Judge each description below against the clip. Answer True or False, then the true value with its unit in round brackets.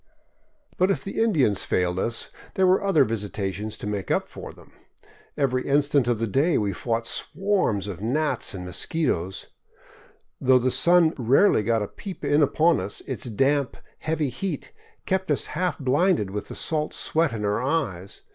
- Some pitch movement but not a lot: False (7.4 semitones)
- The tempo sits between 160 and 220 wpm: True (170 wpm)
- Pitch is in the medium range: False (130 Hz)